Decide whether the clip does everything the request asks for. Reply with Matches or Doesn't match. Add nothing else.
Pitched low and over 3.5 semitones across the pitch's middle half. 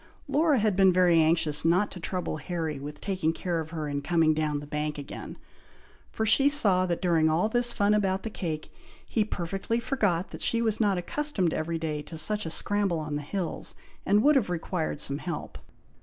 Doesn't match